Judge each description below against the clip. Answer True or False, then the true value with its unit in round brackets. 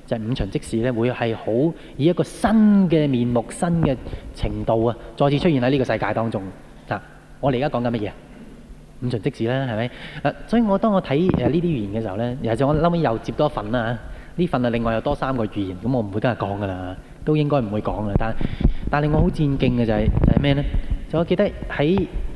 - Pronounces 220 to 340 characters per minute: True (325 characters per minute)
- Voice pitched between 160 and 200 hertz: False (125 Hz)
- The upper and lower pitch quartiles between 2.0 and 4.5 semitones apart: False (5.1 semitones)